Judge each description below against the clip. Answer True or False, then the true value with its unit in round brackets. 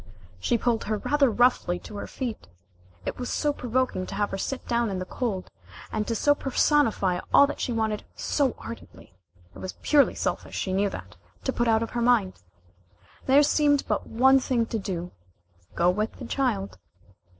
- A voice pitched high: True (230 Hz)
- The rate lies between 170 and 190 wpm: True (185 wpm)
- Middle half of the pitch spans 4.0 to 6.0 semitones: True (4.6 semitones)